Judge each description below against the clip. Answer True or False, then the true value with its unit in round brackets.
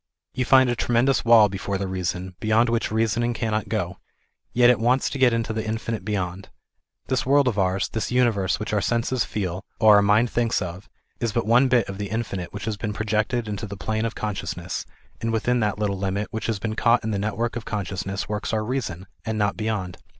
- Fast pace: True (215 wpm)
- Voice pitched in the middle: False (110 Hz)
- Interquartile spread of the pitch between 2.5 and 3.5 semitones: True (3.0 semitones)